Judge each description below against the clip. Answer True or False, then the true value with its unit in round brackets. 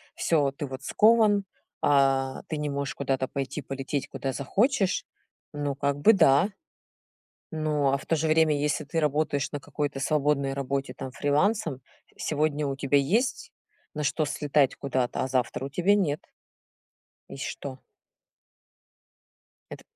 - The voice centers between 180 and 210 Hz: False (145 Hz)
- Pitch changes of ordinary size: False (2.3 semitones)